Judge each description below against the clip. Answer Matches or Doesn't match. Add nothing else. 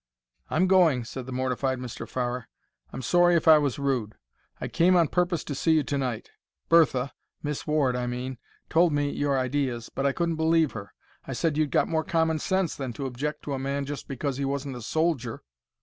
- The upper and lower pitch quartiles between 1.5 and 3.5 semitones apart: Doesn't match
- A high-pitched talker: Doesn't match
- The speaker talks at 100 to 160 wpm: Doesn't match